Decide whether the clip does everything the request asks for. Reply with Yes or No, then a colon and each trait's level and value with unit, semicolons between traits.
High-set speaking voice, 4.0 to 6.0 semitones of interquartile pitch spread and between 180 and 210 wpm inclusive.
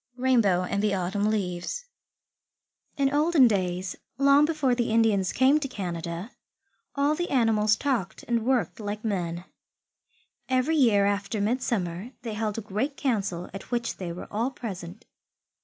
No: high, 220 Hz; average, 5.2 semitones; average, 145 wpm